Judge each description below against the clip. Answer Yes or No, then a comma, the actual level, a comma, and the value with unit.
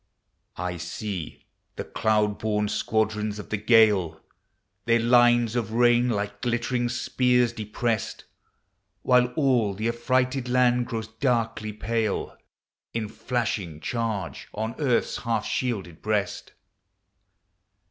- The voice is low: Yes, low, 115 Hz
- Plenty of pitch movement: No, narrow, 2.5 semitones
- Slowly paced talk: Yes, slow, 110 wpm